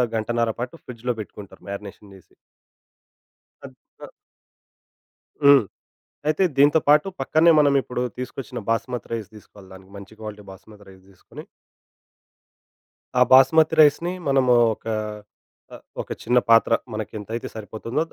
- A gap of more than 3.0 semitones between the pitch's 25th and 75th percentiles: Yes, average, 4.7 semitones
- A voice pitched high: No, low, 115 Hz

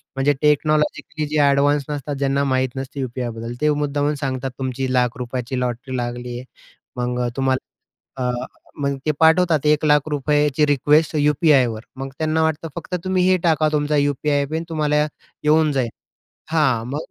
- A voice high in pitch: No, medium, 145 Hz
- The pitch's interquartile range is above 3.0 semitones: No, average, 2.7 semitones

